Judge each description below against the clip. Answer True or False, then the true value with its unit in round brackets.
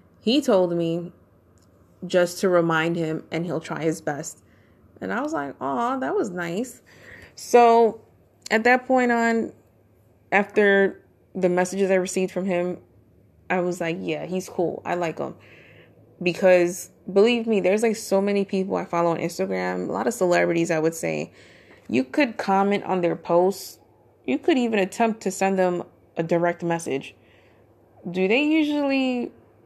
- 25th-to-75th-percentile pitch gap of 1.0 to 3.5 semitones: False (4.3 semitones)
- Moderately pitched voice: True (180 Hz)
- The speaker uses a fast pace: False (160 wpm)